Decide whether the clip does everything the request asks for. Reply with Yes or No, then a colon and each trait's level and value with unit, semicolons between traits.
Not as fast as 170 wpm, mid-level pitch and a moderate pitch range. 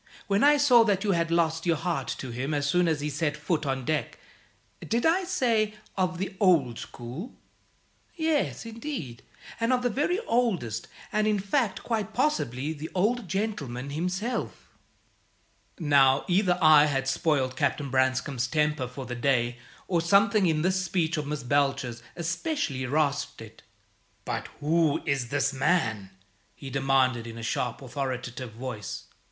No: average, 155 wpm; medium, 155 Hz; wide, 7.0 semitones